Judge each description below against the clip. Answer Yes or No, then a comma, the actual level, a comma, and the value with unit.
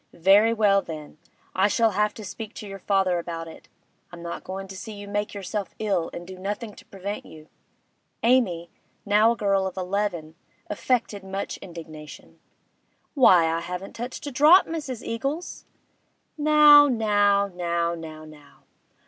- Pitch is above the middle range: Yes, high, 200 Hz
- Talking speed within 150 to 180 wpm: Yes, average, 155 wpm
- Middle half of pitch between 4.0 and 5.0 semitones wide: Yes, average, 4.4 semitones